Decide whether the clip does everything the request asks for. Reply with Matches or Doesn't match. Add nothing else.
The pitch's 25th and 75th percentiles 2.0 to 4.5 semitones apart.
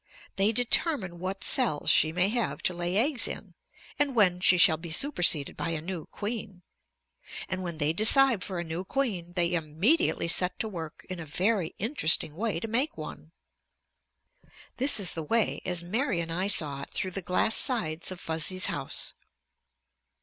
Doesn't match